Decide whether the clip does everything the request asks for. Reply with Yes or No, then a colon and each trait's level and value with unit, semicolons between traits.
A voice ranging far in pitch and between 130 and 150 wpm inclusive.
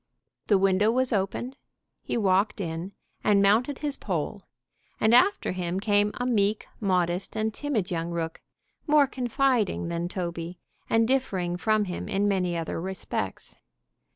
No: average, 4.1 semitones; average, 145 wpm